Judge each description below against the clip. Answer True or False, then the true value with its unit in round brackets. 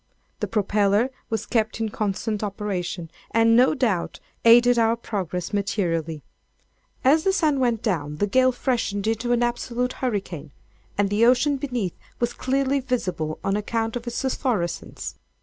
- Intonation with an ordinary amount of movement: True (3.8 semitones)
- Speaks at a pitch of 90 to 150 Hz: False (225 Hz)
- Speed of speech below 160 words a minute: True (150 wpm)